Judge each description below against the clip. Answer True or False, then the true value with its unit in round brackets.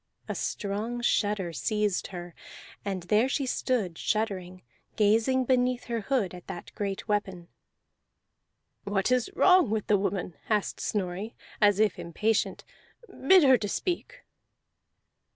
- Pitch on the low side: False (210 Hz)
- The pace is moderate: False (130 wpm)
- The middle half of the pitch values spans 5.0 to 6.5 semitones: False (4.1 semitones)